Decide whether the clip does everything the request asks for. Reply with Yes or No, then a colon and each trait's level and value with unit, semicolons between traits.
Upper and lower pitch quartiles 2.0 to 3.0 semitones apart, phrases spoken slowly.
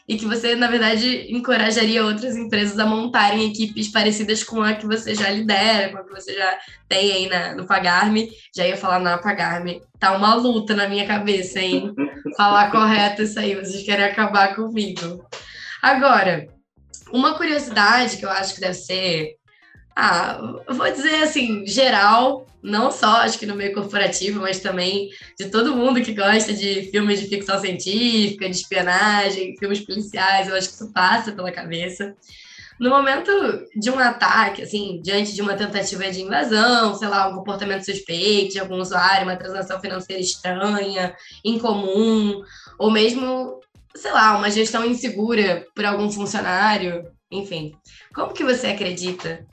No: narrow, 2.6 semitones; average, 160 wpm